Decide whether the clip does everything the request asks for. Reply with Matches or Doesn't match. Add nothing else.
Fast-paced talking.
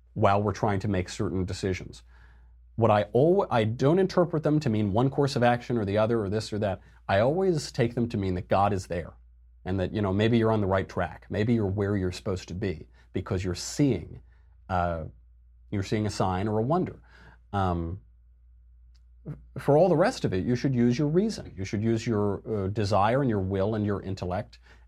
Matches